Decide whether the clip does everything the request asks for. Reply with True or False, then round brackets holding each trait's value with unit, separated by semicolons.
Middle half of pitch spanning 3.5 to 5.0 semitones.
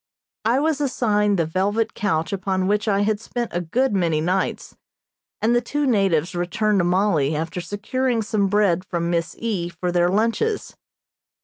True (4.2 semitones)